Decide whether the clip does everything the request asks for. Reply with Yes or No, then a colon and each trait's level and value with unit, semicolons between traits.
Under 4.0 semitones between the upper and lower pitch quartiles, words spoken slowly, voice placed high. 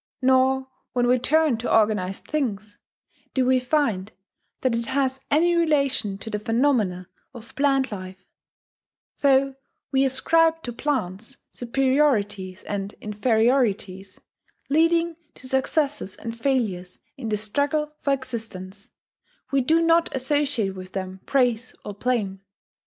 No: average, 5.1 semitones; slow, 125 wpm; very high, 250 Hz